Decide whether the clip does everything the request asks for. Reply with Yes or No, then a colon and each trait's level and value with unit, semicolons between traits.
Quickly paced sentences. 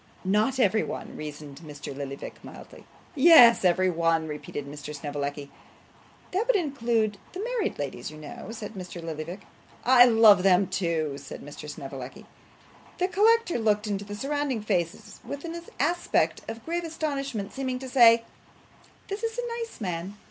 No: average, 155 wpm